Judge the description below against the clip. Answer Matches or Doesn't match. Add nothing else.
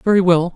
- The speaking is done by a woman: Doesn't match